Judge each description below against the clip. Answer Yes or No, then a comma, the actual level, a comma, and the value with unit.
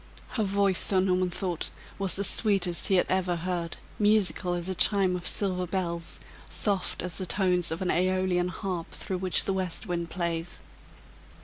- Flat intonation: Yes, narrow, 1.5 semitones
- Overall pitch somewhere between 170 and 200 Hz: Yes, medium, 185 Hz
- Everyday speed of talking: Yes, average, 175 wpm